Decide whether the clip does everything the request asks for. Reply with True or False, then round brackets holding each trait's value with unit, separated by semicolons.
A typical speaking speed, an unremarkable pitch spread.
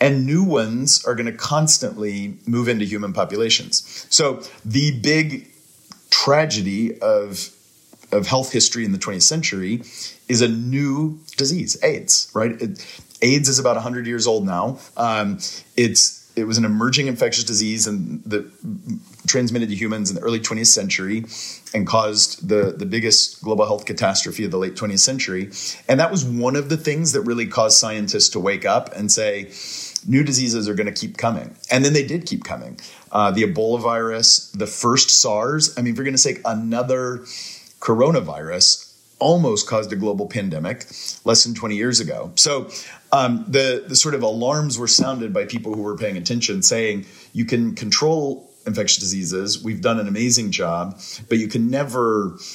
True (170 wpm; 3.8 semitones)